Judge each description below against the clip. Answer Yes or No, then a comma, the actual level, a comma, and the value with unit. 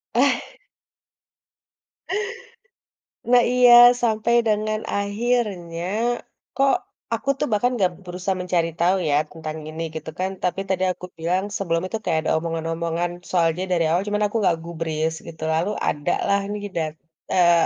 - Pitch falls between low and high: Yes, medium, 180 Hz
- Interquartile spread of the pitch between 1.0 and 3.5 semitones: No, average, 3.9 semitones